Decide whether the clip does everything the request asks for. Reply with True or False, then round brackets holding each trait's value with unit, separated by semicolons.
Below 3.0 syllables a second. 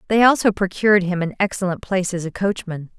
False (6.3 syllables/s)